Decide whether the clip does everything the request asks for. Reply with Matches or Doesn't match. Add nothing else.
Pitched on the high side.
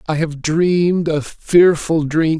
Doesn't match